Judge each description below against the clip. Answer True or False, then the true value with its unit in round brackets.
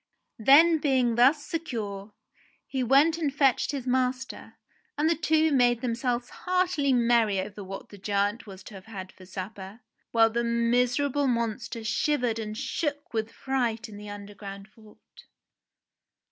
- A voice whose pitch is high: True (235 Hz)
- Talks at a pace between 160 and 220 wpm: False (145 wpm)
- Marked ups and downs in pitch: False (4.5 semitones)